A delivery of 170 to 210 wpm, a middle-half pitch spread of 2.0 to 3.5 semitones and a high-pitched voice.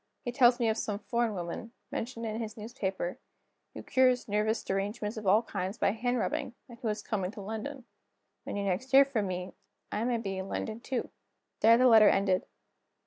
Yes: average, 200 wpm; average, 3.1 semitones; high, 220 Hz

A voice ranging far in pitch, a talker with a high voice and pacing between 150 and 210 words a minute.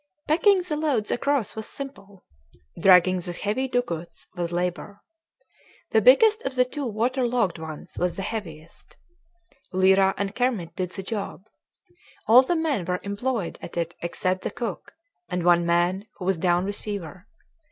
Yes: wide, 5.9 semitones; high, 200 Hz; average, 160 wpm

